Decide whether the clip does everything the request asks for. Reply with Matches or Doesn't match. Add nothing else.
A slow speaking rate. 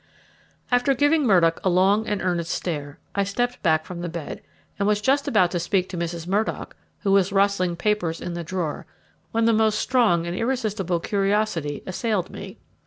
Doesn't match